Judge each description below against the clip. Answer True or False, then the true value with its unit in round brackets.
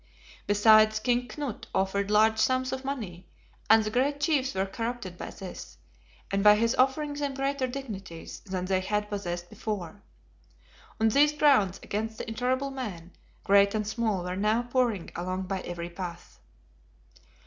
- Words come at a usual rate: True (155 wpm)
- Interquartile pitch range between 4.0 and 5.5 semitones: True (5.1 semitones)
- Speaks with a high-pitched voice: True (215 Hz)